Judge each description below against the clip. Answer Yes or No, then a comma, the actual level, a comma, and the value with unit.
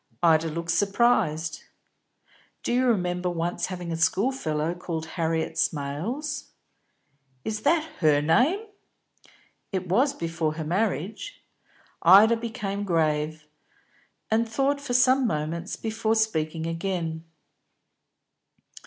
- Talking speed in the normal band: No, slow, 105 wpm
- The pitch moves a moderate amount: No, wide, 5.9 semitones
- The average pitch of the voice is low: No, medium, 180 Hz